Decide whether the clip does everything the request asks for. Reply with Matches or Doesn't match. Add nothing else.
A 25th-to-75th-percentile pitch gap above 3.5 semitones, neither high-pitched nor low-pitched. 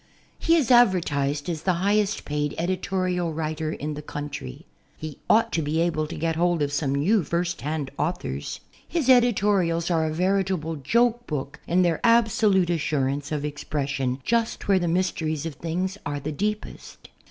Matches